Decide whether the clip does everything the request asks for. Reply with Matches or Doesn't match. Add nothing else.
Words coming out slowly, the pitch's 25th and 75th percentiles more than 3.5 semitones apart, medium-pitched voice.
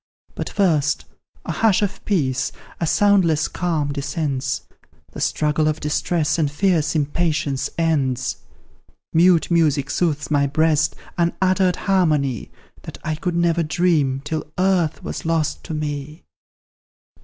Doesn't match